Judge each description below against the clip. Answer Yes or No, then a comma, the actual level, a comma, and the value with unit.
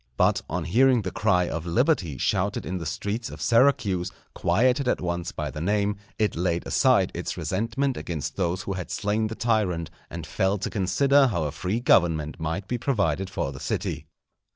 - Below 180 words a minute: No, average, 185 wpm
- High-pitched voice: No, very low, 95 Hz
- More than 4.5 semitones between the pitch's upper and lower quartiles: Yes, average, 4.9 semitones